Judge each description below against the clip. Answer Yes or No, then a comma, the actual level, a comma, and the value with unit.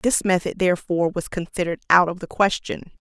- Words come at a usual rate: Yes, average, 175 wpm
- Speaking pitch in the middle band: Yes, medium, 180 Hz